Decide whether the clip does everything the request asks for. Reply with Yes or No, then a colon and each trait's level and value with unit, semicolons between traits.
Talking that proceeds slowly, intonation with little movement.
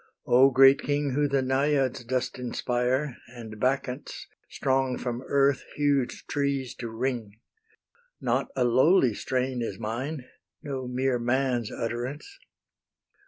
Yes: slow, 120 wpm; narrow, 2.1 semitones